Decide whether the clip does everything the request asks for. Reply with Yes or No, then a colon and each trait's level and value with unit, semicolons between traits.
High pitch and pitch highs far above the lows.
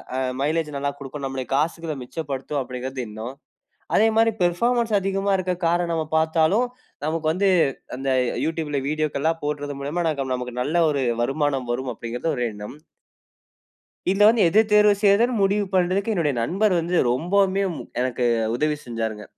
No: medium, 155 Hz; wide, 6.1 semitones